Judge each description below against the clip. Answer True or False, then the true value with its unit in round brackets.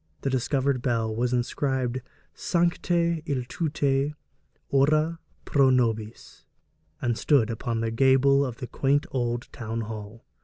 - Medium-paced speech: False (120 wpm)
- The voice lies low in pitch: True (130 Hz)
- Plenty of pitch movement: False (3.3 semitones)